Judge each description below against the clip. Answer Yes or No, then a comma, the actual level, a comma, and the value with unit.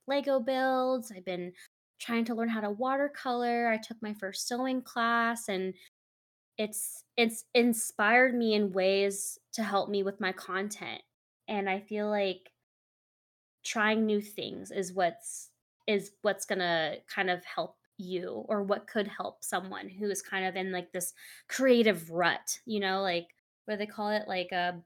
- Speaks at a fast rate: No, average, 165 wpm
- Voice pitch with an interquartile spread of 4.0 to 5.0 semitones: No, average, 3.5 semitones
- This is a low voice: No, high, 205 Hz